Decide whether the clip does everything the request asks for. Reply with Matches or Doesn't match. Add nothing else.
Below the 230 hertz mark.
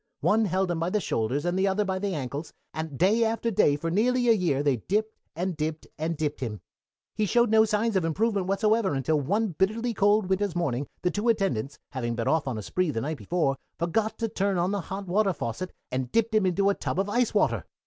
Matches